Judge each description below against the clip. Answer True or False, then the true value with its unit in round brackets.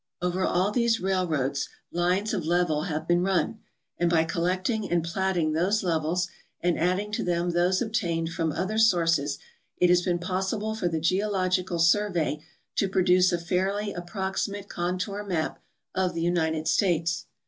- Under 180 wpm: True (155 wpm)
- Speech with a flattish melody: True (2.2 semitones)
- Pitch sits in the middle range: True (180 Hz)